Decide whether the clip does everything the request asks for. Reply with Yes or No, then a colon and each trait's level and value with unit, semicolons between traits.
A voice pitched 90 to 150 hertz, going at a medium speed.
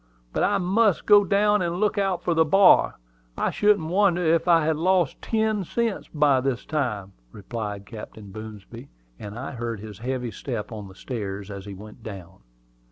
Yes: low, 135 Hz; average, 180 wpm